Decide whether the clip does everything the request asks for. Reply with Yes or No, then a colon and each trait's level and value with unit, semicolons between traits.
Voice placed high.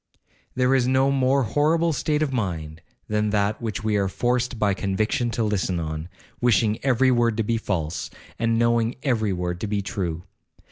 No: low, 110 Hz